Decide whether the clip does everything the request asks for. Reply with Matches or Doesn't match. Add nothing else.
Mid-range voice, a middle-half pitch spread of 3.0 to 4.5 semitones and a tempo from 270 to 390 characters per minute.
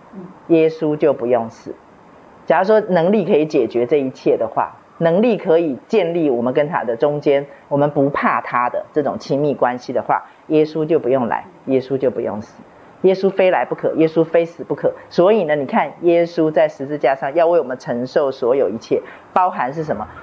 Matches